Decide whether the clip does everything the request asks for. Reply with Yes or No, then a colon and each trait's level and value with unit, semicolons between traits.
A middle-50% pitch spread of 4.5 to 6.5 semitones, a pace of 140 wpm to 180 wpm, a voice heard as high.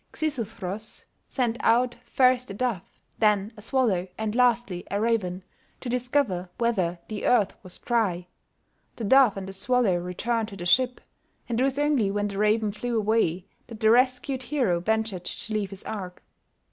No: average, 4.1 semitones; average, 170 wpm; high, 220 Hz